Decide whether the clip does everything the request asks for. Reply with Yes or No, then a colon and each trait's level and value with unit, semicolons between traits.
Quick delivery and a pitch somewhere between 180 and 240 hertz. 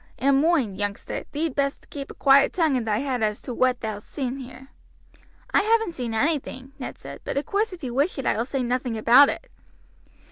No: fast, 215 wpm; very high, 265 Hz